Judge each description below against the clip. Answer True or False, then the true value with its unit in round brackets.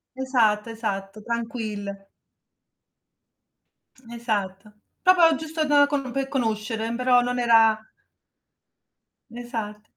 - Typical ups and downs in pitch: True (3.3 semitones)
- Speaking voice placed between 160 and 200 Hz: False (235 Hz)